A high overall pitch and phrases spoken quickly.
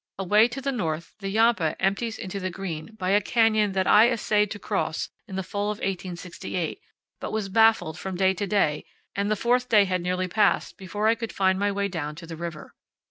Yes: high, 195 Hz; fast, 215 wpm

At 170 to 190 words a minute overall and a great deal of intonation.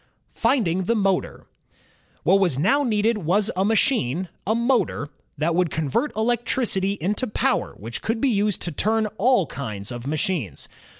No: average, 155 wpm; wide, 5.9 semitones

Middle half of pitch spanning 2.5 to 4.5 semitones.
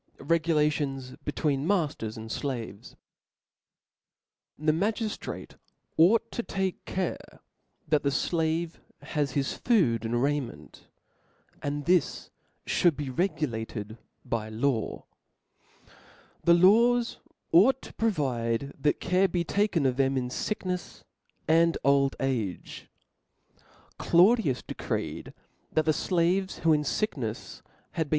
No: average, 5.3 semitones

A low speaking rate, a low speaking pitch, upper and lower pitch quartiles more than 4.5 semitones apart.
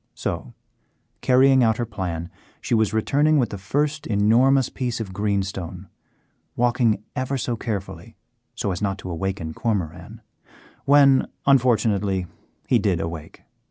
Yes: slow, 130 wpm; low, 110 Hz; average, 5.0 semitones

